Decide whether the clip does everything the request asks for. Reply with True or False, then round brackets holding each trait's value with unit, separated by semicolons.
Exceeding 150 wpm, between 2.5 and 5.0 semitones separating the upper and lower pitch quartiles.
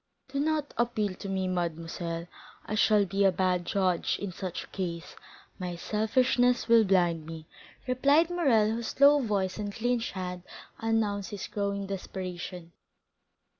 False (145 wpm; 4.2 semitones)